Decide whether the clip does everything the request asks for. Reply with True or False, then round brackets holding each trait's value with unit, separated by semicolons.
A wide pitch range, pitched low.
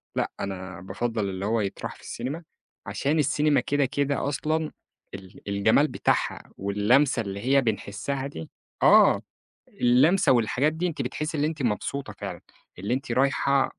True (5.9 semitones; 130 Hz)